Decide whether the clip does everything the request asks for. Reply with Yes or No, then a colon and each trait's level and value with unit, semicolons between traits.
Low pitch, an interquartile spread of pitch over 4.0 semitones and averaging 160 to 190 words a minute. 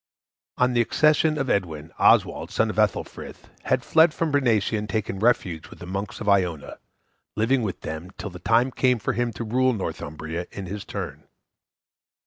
Yes: low, 110 Hz; average, 5.3 semitones; average, 175 wpm